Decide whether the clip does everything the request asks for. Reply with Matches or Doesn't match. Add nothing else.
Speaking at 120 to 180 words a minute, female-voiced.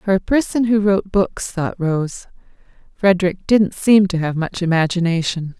Matches